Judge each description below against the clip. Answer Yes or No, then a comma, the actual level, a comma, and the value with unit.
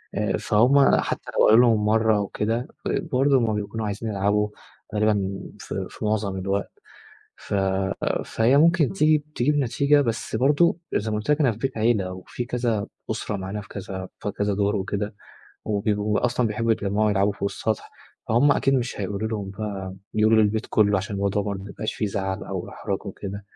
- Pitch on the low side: Yes, low, 105 Hz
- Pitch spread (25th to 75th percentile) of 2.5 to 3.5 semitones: Yes, average, 2.9 semitones